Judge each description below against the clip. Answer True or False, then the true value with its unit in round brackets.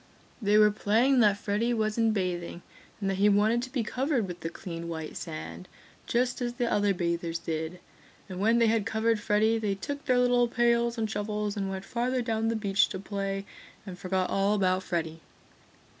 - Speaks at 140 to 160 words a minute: False (195 wpm)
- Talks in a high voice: True (210 Hz)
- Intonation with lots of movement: False (3.7 semitones)